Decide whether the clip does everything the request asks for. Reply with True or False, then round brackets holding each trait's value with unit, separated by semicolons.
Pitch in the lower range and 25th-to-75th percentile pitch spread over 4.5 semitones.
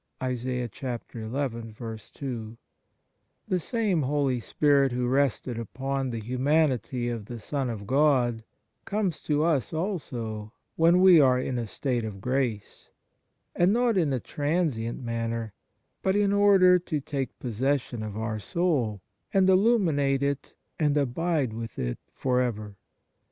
True (130 Hz; 5.1 semitones)